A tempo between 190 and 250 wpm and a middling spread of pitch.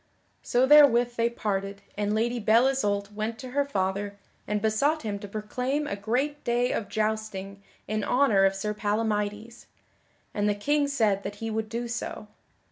No: average, 170 wpm; average, 3.0 semitones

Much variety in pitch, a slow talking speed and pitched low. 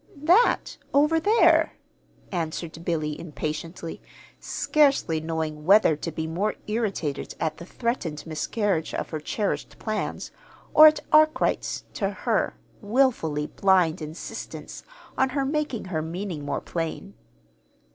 No: wide, 8.2 semitones; slow, 120 wpm; medium, 175 Hz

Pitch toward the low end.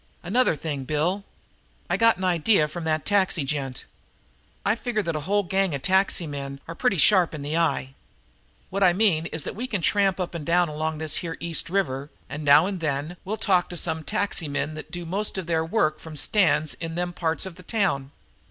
No: medium, 170 Hz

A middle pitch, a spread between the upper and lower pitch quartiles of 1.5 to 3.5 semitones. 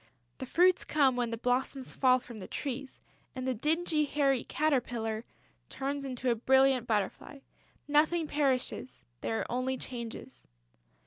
No: very high, 260 Hz; average, 2.7 semitones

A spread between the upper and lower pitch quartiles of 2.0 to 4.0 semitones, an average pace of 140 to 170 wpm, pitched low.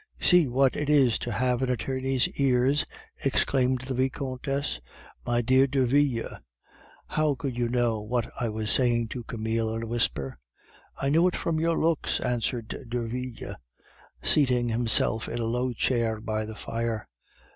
Yes: average, 2.7 semitones; average, 155 wpm; low, 125 Hz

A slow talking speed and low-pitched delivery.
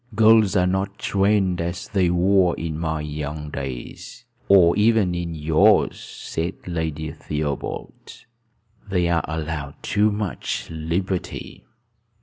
Yes: slow, 120 wpm; very low, 85 Hz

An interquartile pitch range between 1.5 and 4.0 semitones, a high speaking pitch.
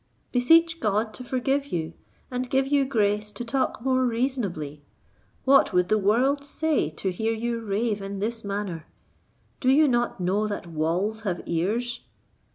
No: average, 4.7 semitones; high, 225 Hz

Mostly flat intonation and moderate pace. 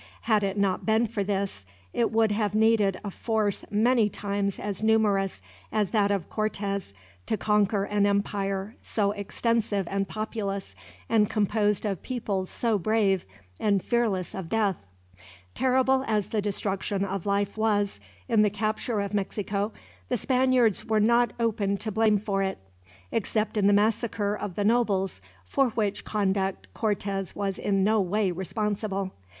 Yes: narrow, 1.8 semitones; average, 155 wpm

